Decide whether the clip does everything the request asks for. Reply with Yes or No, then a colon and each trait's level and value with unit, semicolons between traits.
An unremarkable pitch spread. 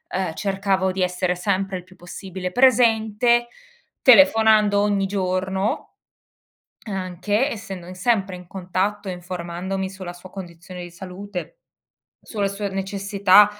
No: narrow, 2.0 semitones